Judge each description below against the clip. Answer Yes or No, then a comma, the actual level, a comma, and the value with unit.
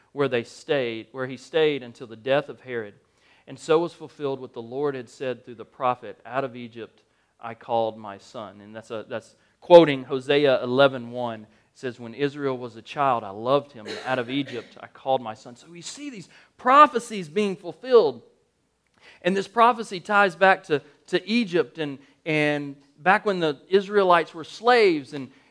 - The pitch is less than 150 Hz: Yes, medium, 140 Hz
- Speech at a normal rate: Yes, average, 190 wpm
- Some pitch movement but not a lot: No, wide, 5.8 semitones